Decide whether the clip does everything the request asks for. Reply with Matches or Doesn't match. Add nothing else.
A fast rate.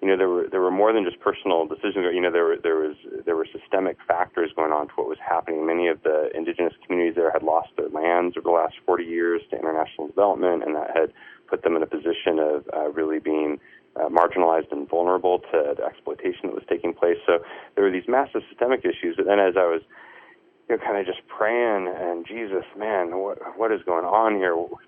Matches